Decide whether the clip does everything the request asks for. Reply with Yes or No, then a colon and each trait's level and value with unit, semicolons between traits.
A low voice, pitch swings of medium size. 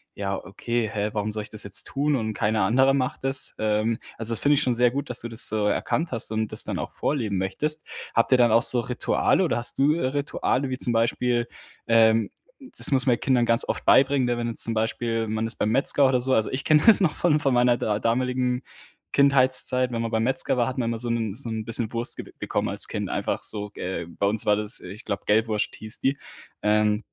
Yes: low, 115 Hz; average, 3.1 semitones